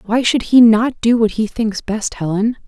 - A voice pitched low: No, high, 225 Hz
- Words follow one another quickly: Yes, fast, 225 wpm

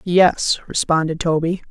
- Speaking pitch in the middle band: Yes, medium, 170 Hz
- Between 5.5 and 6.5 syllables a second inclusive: No, 4.1 syllables/s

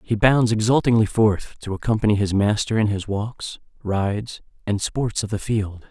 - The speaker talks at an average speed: Yes, average, 175 wpm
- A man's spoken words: Yes, male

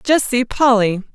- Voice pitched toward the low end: No, high, 240 Hz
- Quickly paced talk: No, average, 155 wpm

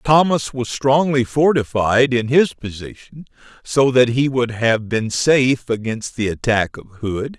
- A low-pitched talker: Yes, low, 125 Hz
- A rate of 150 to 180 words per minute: Yes, average, 155 wpm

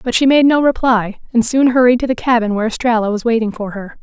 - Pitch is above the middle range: Yes, high, 235 Hz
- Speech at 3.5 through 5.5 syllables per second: No, 6.4 syllables/s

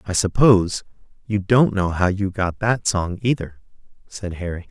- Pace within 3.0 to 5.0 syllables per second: Yes, 4.6 syllables/s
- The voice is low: Yes, low, 100 Hz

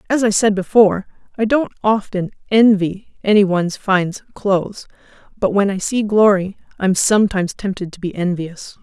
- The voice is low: No, high, 200 Hz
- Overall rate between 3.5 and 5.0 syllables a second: No, 5.2 syllables/s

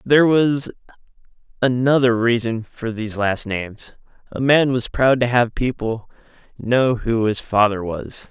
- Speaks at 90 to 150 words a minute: Yes, average, 145 wpm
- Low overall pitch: Yes, low, 120 Hz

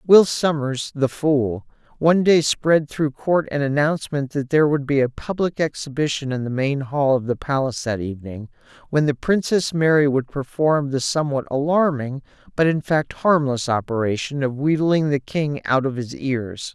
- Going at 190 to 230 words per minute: No, average, 175 wpm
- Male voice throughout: Yes, male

